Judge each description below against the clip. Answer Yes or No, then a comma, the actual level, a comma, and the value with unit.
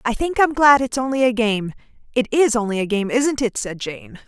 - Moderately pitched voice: No, high, 235 Hz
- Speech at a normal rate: No, fast, 240 wpm